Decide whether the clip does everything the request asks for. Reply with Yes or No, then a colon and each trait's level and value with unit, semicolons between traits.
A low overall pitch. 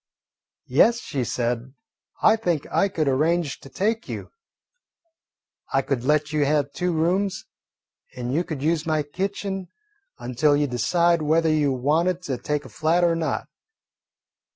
No: medium, 155 Hz